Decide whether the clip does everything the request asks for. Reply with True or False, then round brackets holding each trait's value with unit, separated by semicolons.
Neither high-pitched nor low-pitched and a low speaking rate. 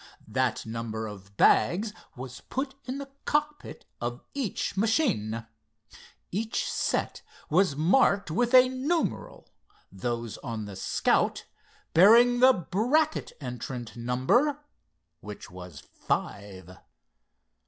True (165 Hz; 105 wpm)